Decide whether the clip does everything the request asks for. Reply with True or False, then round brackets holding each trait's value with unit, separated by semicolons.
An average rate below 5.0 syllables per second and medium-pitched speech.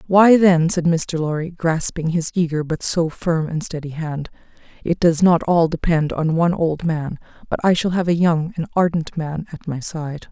True (4.6 syllables/s; 165 Hz)